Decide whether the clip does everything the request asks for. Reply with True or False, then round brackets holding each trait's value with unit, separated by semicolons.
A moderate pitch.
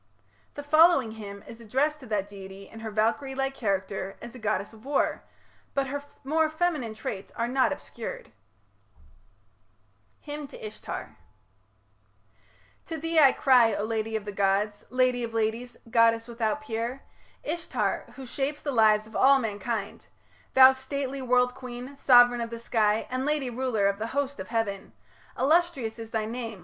False (240 Hz)